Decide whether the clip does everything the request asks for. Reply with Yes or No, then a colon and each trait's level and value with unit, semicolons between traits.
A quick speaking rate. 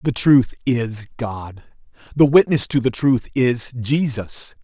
No: average, 140 wpm